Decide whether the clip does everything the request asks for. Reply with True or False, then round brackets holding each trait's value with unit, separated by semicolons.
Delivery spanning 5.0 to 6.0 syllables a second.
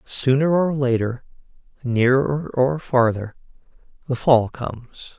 False (3.7 syllables/s)